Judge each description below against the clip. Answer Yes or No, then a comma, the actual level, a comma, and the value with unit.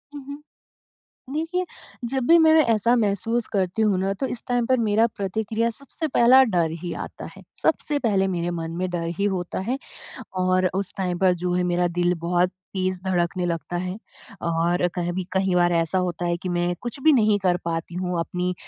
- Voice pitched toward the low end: No, medium, 185 Hz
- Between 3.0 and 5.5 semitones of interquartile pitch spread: Yes, average, 4.6 semitones